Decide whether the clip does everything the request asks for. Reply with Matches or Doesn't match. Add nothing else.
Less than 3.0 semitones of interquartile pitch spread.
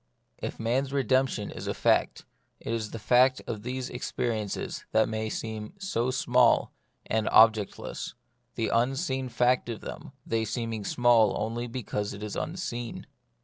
Matches